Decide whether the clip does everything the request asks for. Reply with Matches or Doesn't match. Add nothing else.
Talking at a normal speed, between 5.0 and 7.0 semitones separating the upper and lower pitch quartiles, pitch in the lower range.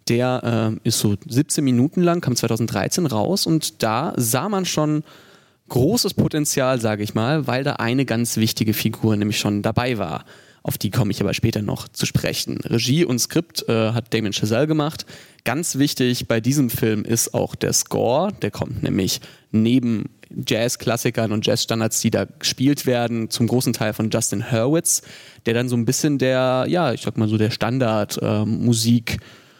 Doesn't match